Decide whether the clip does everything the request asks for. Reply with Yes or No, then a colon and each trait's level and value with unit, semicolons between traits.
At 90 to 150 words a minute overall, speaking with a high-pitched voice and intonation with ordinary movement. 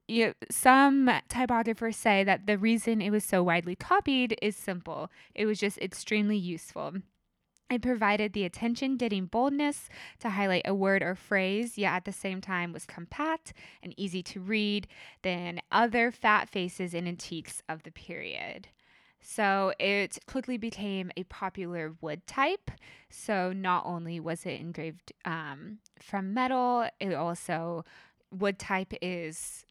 Yes: average, 145 wpm; high, 195 Hz; average, 4.2 semitones